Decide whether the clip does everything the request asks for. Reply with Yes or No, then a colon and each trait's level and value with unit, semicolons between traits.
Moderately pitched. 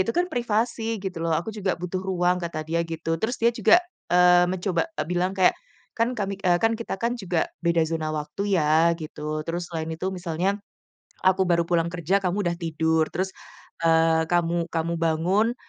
Yes: medium, 175 Hz